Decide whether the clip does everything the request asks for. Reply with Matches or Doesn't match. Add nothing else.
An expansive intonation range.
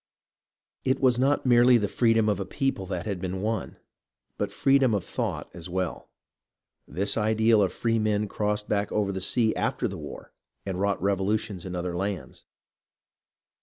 Doesn't match